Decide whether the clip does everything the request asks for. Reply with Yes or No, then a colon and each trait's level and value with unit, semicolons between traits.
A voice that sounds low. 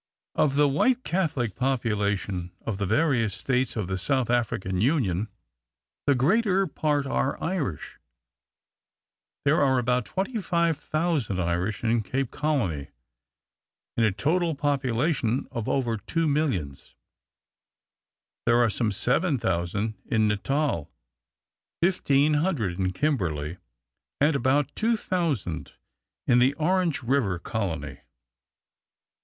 Yes: low, 125 Hz